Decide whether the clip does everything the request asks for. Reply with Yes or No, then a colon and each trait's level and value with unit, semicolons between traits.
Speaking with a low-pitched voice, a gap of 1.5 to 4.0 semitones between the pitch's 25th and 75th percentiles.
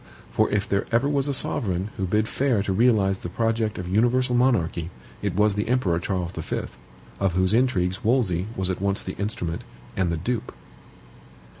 No: low, 100 Hz; average, 4.4 semitones